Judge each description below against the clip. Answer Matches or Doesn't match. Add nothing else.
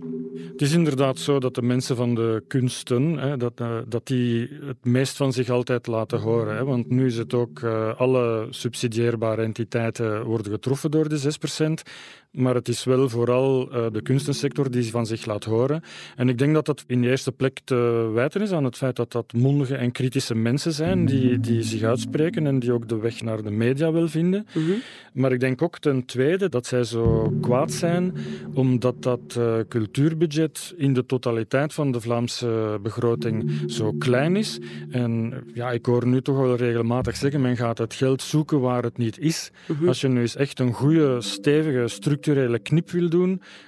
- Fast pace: Doesn't match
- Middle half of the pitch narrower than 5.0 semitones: Matches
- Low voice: Matches